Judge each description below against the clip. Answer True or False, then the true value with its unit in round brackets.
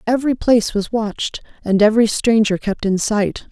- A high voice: True (215 Hz)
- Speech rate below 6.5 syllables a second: True (5.4 syllables/s)